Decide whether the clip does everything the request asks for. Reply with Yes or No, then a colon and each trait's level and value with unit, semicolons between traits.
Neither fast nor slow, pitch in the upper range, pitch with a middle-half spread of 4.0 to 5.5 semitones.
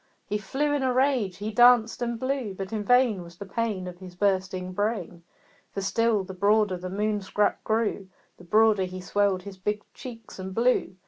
No: average, 195 wpm; high, 205 Hz; average, 3.5 semitones